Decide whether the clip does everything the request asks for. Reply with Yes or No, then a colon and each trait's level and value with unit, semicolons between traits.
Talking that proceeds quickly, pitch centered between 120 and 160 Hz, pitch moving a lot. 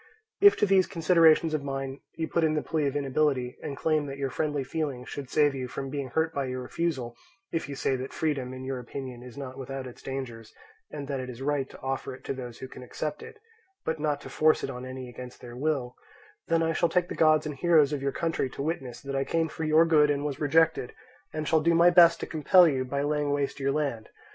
No: fast, 245 wpm; medium, 140 Hz; average, 3.2 semitones